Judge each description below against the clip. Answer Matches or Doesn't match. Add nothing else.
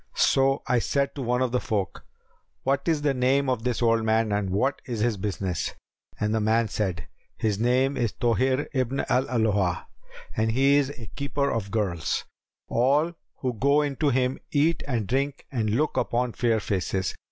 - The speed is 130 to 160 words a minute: Doesn't match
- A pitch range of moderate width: Matches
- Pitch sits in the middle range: Doesn't match